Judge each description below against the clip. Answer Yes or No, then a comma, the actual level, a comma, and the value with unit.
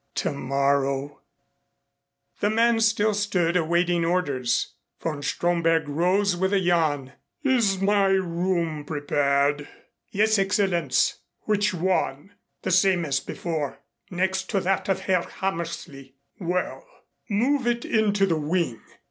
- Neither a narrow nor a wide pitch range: Yes, average, 4.9 semitones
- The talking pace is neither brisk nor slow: No, slow, 115 wpm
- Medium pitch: Yes, medium, 175 Hz